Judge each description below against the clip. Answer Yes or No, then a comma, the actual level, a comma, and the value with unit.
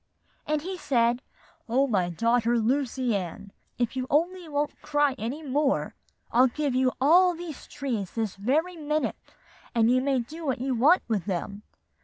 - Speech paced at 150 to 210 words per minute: Yes, average, 170 wpm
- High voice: Yes, very high, 260 Hz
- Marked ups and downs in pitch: No, average, 4.5 semitones